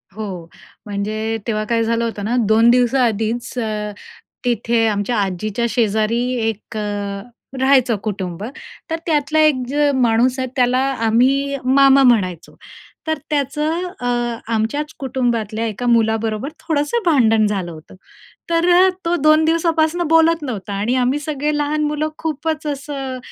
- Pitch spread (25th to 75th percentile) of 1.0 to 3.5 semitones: No, average, 5.2 semitones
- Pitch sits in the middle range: No, high, 245 Hz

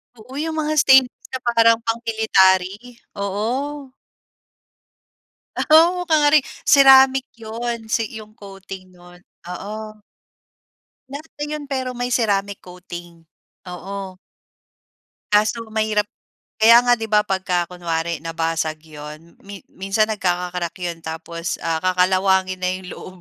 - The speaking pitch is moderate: No, high, 205 Hz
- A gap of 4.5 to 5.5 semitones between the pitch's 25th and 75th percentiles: Yes, average, 5.1 semitones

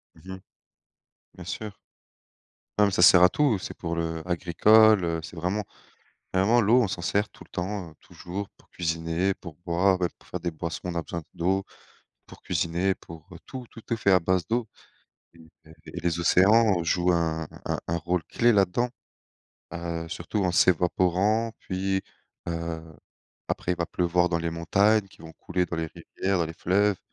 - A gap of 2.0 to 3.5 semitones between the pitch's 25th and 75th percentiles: Yes, average, 2.9 semitones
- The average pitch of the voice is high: No, very low, 90 Hz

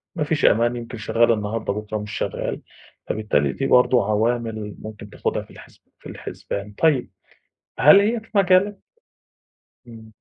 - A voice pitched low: Yes, low, 115 Hz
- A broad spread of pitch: Yes, wide, 5.7 semitones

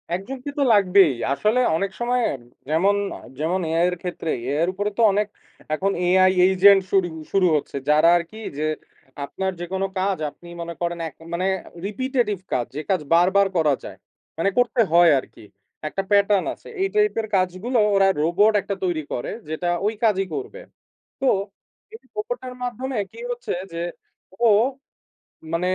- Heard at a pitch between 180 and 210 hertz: Yes, high, 190 Hz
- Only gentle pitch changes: No, average, 4.1 semitones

